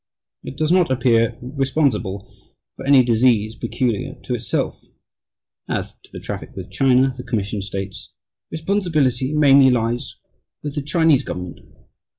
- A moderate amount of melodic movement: Yes, average, 3.7 semitones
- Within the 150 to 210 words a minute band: No, slow, 135 wpm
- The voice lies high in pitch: No, low, 130 Hz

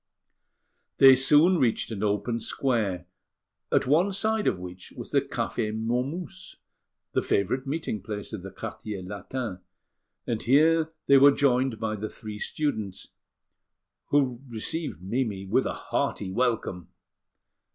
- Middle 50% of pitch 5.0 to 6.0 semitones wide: Yes, average, 5.3 semitones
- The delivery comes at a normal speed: No, slow, 130 wpm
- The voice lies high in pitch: No, low, 120 Hz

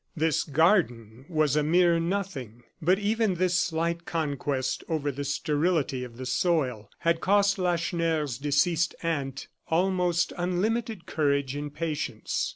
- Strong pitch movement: No, average, 3.9 semitones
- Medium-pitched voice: Yes, medium, 160 Hz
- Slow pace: Yes, slow, 130 wpm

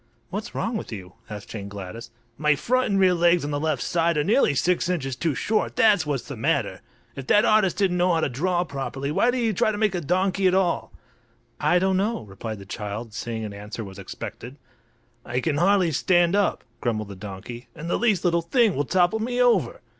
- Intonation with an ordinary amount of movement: No, wide, 8.2 semitones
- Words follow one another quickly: Yes, fast, 220 wpm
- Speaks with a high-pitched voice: No, medium, 170 Hz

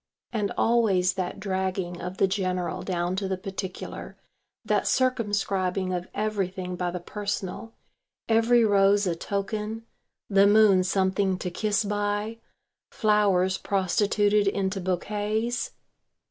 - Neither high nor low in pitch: No, high, 195 Hz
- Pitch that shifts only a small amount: Yes, narrow, 2.2 semitones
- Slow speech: Yes, slow, 120 wpm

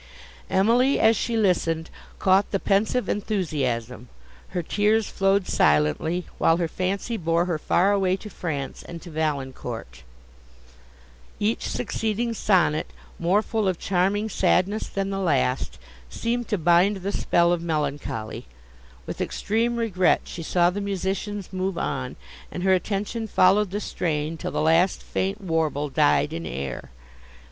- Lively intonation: No, average, 4.1 semitones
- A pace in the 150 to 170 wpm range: No, average, 140 wpm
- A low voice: No, medium, 185 Hz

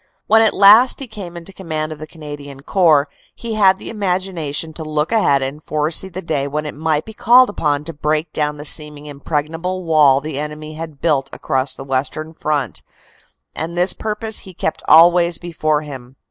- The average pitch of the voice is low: No, medium, 155 Hz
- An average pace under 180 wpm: No, average, 190 wpm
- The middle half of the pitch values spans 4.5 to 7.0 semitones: No, average, 3.4 semitones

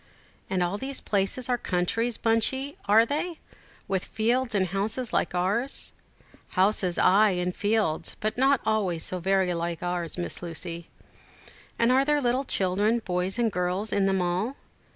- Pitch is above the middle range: Yes, high, 205 Hz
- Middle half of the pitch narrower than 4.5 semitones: No, average, 4.8 semitones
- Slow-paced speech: No, average, 155 wpm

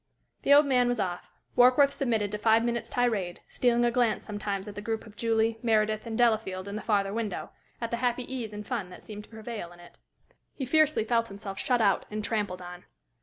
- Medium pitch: No, high, 220 Hz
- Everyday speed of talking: No, fast, 220 wpm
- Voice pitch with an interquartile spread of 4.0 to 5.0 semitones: No, average, 2.8 semitones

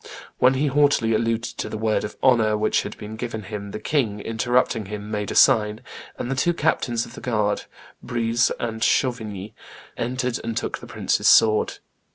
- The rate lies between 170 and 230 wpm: Yes, average, 185 wpm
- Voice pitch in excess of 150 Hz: No, low, 115 Hz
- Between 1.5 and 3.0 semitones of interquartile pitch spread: Yes, narrow, 2.4 semitones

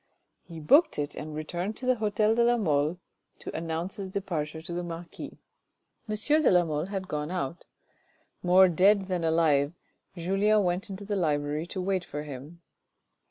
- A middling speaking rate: Yes, average, 170 wpm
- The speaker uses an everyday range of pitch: Yes, average, 4.1 semitones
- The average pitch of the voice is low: No, medium, 175 Hz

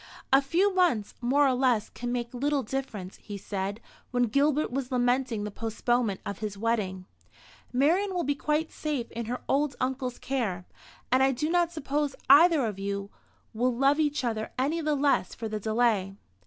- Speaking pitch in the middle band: No, very high, 250 Hz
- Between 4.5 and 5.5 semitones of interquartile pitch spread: Yes, average, 4.8 semitones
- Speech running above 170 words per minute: Yes, average, 180 wpm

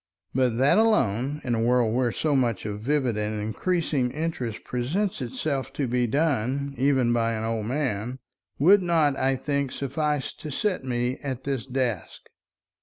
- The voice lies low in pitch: Yes, low, 130 Hz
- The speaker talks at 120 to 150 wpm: No, average, 165 wpm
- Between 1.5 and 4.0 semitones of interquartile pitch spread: Yes, average, 3.5 semitones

